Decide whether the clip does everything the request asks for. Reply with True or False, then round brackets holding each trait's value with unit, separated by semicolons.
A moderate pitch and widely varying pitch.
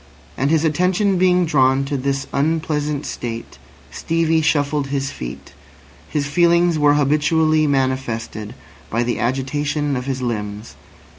False (145 Hz; 3.2 semitones)